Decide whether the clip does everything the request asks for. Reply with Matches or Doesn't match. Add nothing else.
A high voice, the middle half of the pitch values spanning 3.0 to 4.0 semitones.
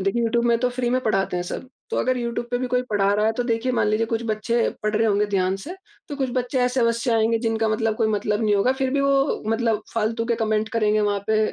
Doesn't match